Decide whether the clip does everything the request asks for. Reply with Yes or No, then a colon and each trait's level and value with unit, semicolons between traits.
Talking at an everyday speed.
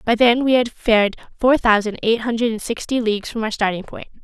No: fast, 215 wpm